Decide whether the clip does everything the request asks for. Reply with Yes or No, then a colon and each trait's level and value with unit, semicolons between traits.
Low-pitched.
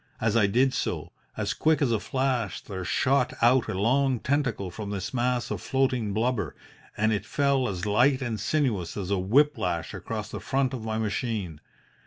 Yes: low, 115 Hz